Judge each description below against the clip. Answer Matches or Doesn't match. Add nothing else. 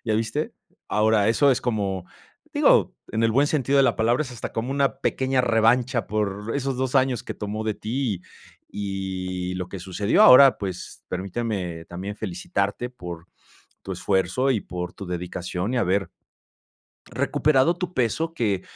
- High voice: Doesn't match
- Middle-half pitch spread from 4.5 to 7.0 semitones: Matches